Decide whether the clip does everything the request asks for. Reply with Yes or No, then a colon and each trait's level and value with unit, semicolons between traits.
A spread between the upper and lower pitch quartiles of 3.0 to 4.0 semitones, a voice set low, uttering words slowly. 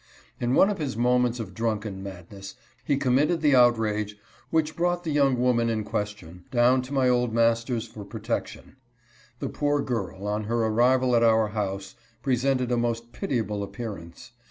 No: average, 3.3 semitones; low, 115 Hz; average, 165 wpm